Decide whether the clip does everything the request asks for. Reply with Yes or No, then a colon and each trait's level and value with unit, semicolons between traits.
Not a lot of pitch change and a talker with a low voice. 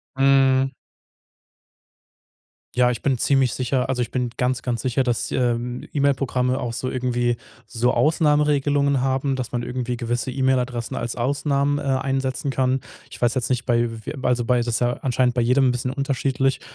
Yes: narrow, 1.7 semitones; low, 130 Hz